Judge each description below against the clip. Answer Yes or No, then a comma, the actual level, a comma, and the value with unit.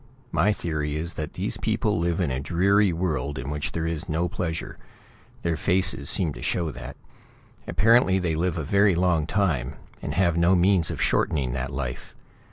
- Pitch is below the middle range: Yes, very low, 85 Hz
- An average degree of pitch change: Yes, average, 3.7 semitones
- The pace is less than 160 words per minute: No, average, 180 wpm